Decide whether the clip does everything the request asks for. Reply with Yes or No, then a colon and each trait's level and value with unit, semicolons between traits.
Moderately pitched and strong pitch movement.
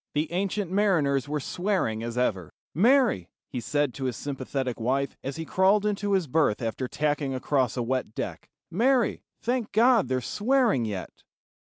Yes: medium, 145 Hz; wide, 8.0 semitones